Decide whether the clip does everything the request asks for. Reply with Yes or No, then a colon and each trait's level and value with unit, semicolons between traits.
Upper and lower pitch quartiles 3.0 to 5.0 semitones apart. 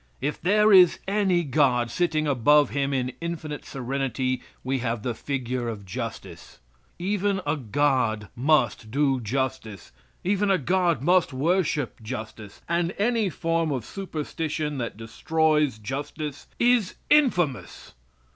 No: wide, 5.5 semitones